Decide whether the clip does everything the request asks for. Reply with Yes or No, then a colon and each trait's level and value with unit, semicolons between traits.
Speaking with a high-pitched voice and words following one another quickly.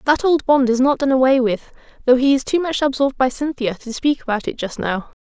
Yes: very high, 260 Hz; fast, 250 wpm